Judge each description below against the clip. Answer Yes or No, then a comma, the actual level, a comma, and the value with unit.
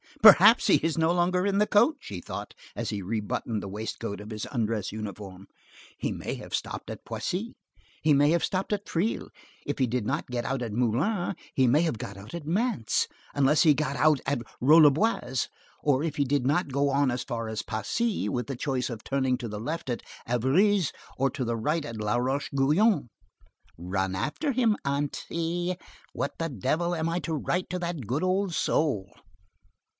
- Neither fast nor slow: Yes, average, 190 wpm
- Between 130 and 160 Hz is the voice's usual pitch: Yes, medium, 140 Hz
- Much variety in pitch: Yes, wide, 6.6 semitones